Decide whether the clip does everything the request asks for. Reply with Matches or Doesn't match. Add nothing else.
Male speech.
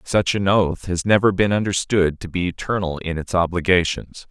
Matches